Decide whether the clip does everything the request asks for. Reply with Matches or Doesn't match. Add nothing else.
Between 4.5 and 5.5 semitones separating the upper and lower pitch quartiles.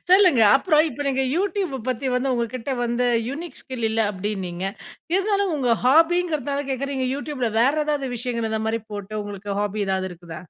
Matches